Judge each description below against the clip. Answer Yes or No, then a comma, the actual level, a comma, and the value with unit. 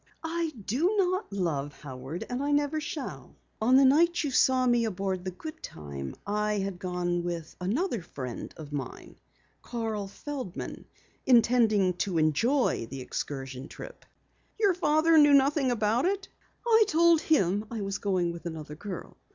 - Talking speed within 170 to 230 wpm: No, average, 150 wpm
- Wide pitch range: Yes, wide, 9.0 semitones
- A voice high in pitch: Yes, high, 215 Hz